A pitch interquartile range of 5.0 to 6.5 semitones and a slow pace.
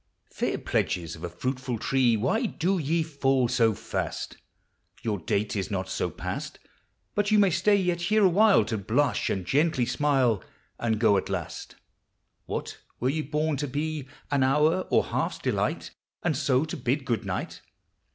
No: wide, 5.5 semitones; average, 170 wpm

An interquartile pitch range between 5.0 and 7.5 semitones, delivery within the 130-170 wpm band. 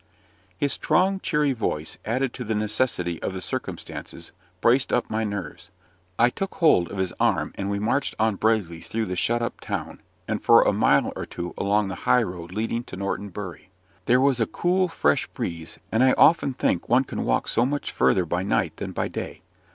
No: wide, 5.5 semitones; average, 200 wpm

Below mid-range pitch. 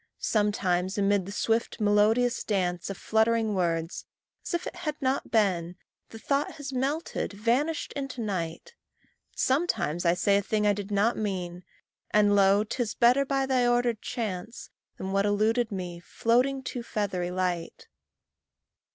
No: high, 210 Hz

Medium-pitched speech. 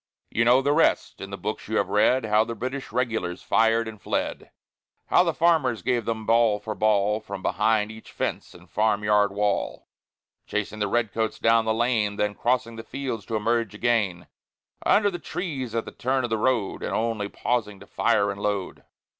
No: low, 110 Hz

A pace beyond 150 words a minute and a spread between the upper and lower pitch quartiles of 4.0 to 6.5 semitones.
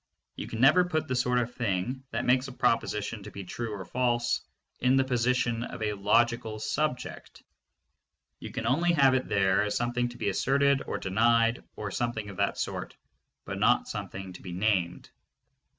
No: average, 180 wpm; average, 3.5 semitones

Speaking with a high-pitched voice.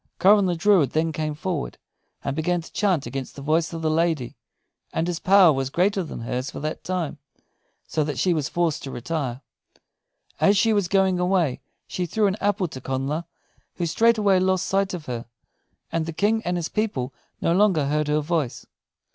No: medium, 165 Hz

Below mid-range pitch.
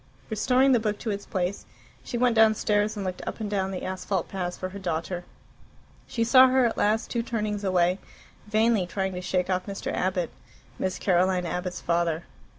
No: high, 195 Hz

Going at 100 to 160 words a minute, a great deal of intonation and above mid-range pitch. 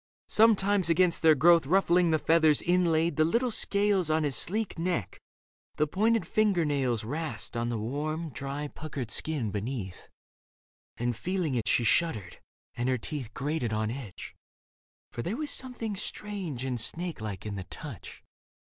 No: average, 155 wpm; wide, 6.9 semitones; medium, 155 Hz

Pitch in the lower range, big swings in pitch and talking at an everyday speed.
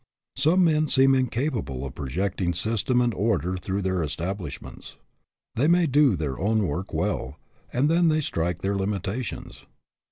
Yes: low, 100 Hz; wide, 7.2 semitones; average, 150 wpm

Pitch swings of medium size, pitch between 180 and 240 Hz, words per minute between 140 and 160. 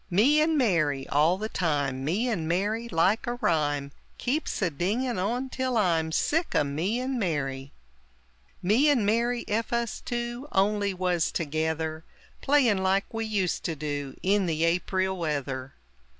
No: wide, 6.8 semitones; high, 190 Hz; average, 155 wpm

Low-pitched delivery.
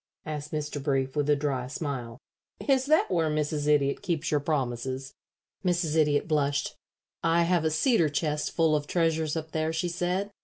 No: medium, 155 Hz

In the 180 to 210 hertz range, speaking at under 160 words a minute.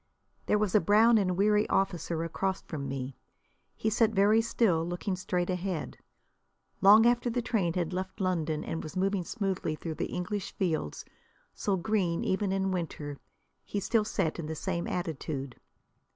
No: medium, 185 Hz; average, 165 wpm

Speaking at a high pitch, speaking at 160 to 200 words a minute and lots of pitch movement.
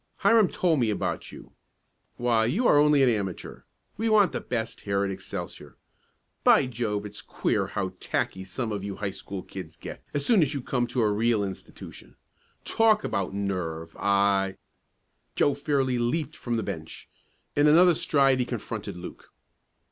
No: low, 115 Hz; average, 170 wpm; wide, 6.5 semitones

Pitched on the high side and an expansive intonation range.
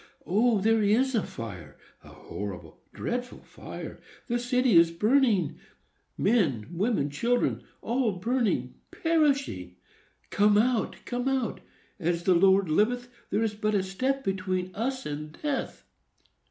Yes: high, 210 Hz; wide, 5.7 semitones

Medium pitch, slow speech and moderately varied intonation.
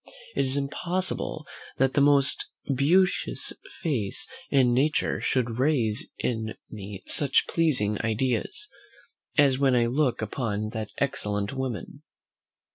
No: low, 130 Hz; slow, 120 wpm; average, 4.3 semitones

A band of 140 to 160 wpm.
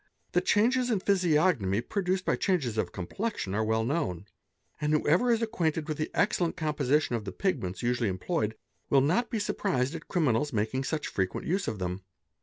No: average, 185 wpm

